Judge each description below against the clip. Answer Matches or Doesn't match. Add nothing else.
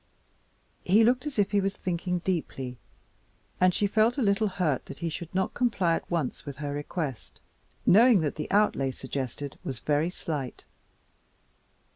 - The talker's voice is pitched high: Doesn't match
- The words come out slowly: Doesn't match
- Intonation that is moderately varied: Doesn't match